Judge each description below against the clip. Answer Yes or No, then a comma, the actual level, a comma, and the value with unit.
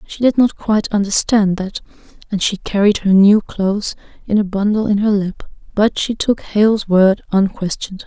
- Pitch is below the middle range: No, high, 205 Hz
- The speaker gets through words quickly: No, average, 180 wpm